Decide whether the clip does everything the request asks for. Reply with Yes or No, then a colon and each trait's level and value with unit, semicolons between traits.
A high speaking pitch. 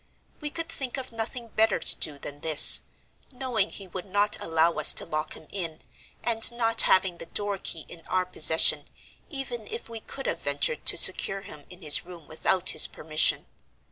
Yes: high, 195 Hz